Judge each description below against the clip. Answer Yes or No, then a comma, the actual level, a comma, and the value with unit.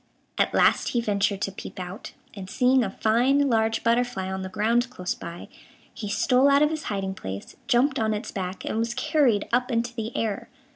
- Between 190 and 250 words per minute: Yes, average, 200 wpm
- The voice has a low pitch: No, high, 225 Hz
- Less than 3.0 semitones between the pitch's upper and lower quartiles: No, average, 4.1 semitones